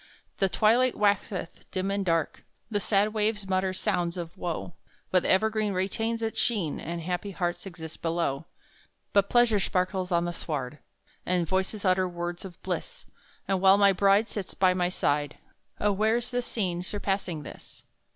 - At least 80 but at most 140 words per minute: No, average, 165 wpm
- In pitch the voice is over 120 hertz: Yes, high, 190 Hz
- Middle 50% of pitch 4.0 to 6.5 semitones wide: No, average, 3.0 semitones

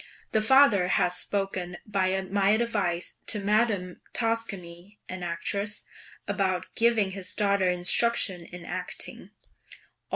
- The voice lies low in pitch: No, high, 195 Hz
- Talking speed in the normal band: No, slow, 110 wpm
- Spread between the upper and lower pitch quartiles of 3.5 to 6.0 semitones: No, average, 3.0 semitones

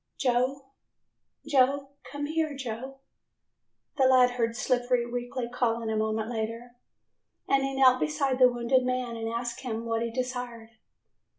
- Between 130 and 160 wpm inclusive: Yes, average, 140 wpm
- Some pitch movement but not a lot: No, narrow, 2.3 semitones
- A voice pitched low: No, high, 245 Hz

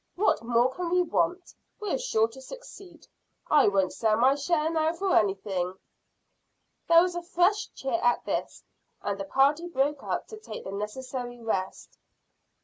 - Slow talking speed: No, average, 160 wpm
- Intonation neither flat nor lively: No, wide, 7.8 semitones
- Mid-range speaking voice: No, very high, 275 Hz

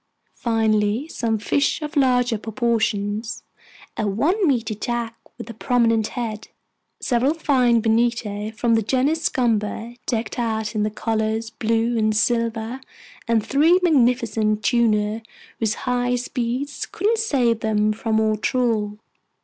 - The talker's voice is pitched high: Yes, high, 230 Hz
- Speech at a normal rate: No, slow, 130 wpm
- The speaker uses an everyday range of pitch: No, narrow, 2.3 semitones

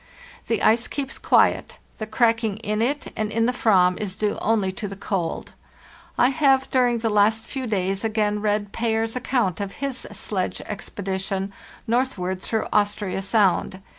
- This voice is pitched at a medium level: No, high, 215 Hz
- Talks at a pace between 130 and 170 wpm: Yes, average, 160 wpm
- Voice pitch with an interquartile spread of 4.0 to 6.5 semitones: No, average, 2.9 semitones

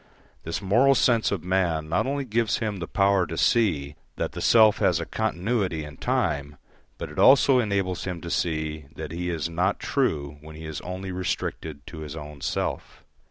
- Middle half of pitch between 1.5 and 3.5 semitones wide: No, average, 5.1 semitones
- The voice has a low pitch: Yes, very low, 90 Hz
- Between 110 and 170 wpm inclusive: No, average, 190 wpm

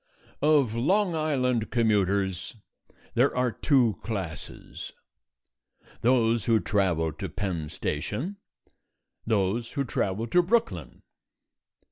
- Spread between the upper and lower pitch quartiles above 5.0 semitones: Yes, wide, 5.4 semitones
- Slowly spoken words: Yes, slow, 95 wpm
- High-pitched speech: No, low, 115 Hz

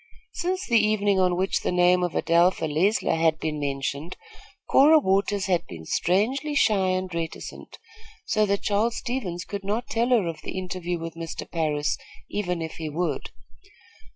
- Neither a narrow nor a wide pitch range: Yes, average, 4.0 semitones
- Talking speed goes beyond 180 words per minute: No, average, 165 wpm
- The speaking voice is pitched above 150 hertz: Yes, medium, 185 Hz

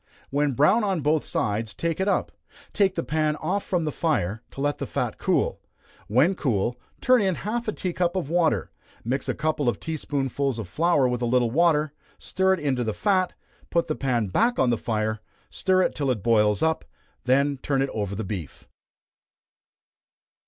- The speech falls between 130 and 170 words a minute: No, average, 195 wpm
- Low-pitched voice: No, medium, 145 Hz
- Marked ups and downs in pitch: Yes, wide, 6.3 semitones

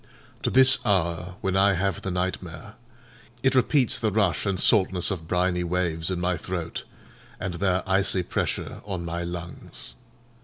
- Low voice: Yes, very low, 90 Hz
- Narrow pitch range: Yes, narrow, 2.1 semitones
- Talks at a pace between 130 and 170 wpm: Yes, average, 155 wpm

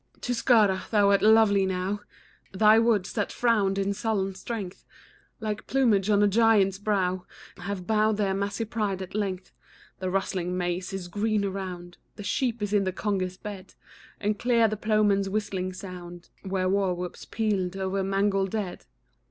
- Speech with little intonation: Yes, narrow, 2.2 semitones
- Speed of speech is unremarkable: Yes, average, 160 wpm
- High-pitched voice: Yes, high, 200 Hz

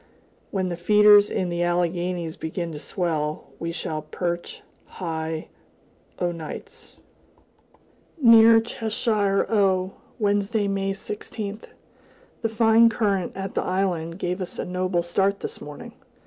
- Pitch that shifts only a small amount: No, average, 3.2 semitones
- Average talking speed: No, slow, 125 wpm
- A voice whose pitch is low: No, medium, 185 Hz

